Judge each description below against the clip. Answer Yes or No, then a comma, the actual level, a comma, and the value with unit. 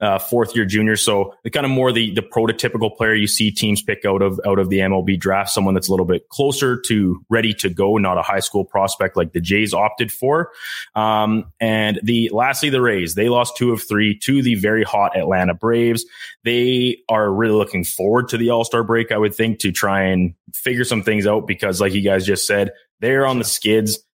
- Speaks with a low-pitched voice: Yes, low, 110 Hz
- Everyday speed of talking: No, fast, 225 wpm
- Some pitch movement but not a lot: Yes, average, 3.0 semitones